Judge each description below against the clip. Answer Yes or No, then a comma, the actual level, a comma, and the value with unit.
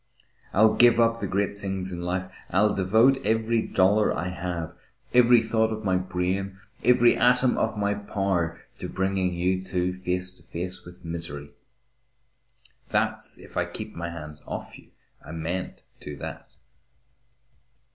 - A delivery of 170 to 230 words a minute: No, average, 150 wpm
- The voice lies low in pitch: Yes, very low, 95 Hz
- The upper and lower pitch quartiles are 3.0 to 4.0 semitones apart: Yes, average, 3.5 semitones